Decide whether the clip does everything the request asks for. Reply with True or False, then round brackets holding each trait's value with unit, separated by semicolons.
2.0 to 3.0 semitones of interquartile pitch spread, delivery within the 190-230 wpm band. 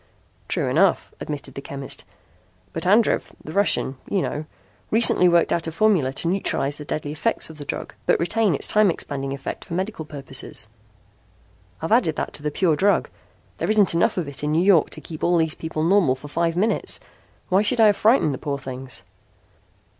False (5.3 semitones; 195 wpm)